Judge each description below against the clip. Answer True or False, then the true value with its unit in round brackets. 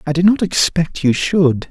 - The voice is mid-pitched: True (165 Hz)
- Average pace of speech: False (210 wpm)